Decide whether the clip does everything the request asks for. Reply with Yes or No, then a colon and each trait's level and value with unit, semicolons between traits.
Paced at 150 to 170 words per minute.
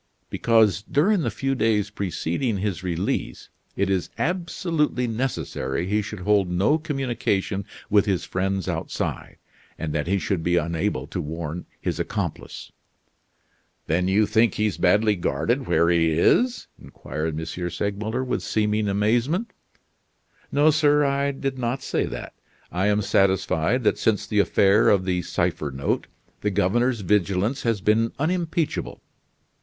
No: average, 140 wpm